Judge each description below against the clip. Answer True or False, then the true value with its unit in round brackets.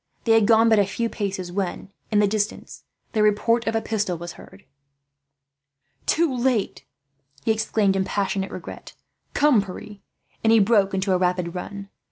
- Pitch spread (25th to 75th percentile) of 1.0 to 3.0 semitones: True (2.6 semitones)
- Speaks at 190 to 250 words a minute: False (170 wpm)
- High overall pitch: True (205 Hz)